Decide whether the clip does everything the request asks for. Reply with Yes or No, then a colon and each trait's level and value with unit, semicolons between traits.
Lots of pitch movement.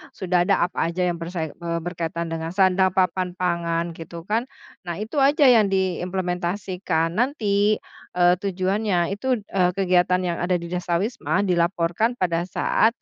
No: narrow, 2.5 semitones